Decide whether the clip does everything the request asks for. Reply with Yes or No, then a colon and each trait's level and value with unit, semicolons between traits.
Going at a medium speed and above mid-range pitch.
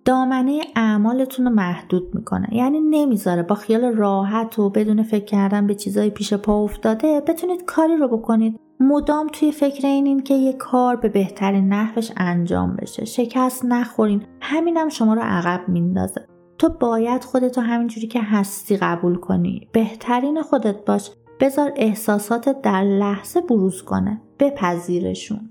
Yes: average, 145 wpm; high, 225 Hz